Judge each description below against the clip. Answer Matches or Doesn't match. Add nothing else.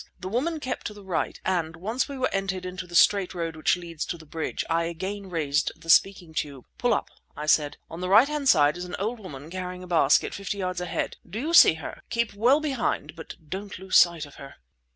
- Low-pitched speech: Doesn't match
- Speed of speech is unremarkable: Doesn't match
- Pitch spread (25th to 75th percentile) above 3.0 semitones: Matches